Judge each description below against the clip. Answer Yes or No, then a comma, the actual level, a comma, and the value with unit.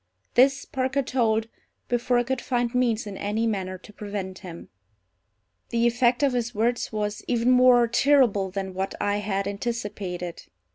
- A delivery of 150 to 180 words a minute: Yes, average, 155 wpm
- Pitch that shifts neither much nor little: Yes, average, 3.5 semitones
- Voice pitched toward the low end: No, high, 230 Hz